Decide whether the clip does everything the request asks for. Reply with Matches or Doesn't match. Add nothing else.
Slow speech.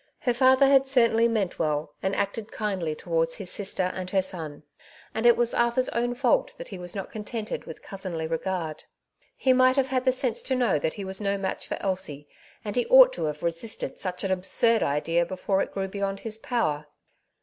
Doesn't match